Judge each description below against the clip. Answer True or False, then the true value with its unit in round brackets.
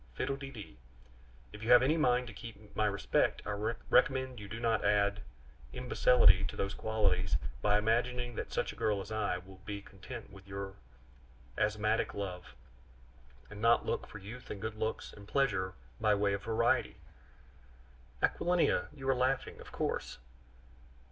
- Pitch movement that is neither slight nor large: True (3.5 semitones)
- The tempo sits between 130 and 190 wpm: True (170 wpm)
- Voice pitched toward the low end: True (105 Hz)